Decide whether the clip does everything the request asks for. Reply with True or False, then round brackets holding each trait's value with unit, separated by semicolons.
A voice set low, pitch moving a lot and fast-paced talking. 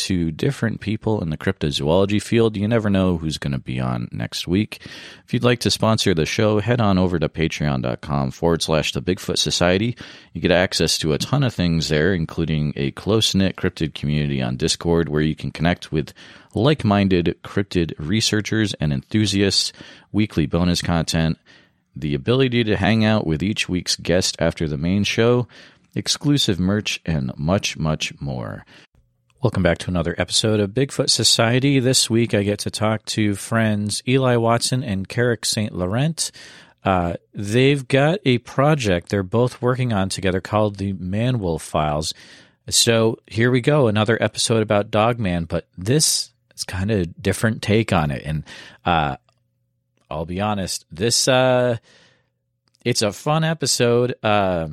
False (105 Hz; 5.7 semitones; 165 wpm)